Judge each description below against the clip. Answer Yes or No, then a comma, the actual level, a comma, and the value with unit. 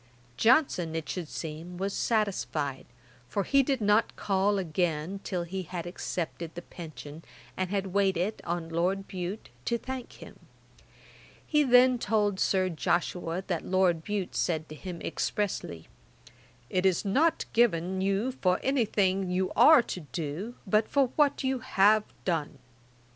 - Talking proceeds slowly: No, average, 145 wpm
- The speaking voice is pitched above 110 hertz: Yes, high, 190 Hz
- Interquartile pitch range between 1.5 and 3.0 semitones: No, average, 3.9 semitones